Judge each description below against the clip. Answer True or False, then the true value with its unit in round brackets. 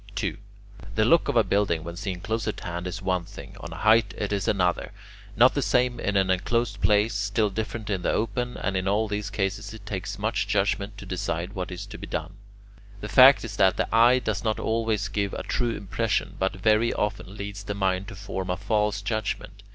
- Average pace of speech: False (220 wpm)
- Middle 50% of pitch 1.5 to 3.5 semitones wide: True (2.4 semitones)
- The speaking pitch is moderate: False (100 Hz)